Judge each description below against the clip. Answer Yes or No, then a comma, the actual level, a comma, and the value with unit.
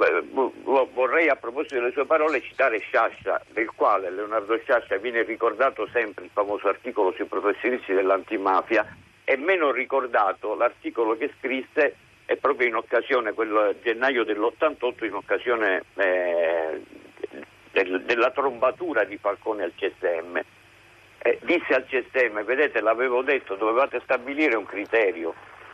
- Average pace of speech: Yes, average, 125 wpm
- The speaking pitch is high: Yes, very high, 315 Hz